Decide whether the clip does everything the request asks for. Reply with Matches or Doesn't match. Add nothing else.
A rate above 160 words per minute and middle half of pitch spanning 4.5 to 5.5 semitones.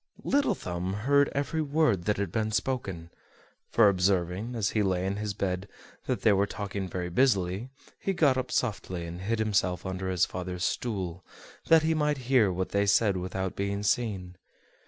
Matches